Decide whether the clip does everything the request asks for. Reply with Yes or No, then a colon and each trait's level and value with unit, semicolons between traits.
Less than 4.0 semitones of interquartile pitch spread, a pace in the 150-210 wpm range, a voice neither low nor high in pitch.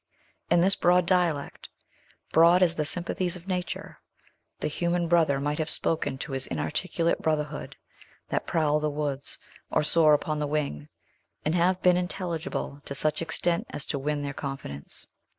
Yes: average, 3.1 semitones; average, 160 wpm; medium, 155 Hz